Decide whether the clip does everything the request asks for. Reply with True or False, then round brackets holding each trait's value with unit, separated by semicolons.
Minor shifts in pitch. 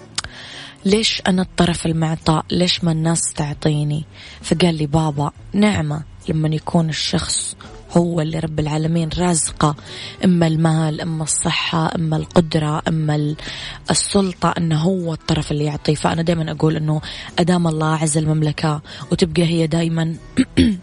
True (2.1 semitones)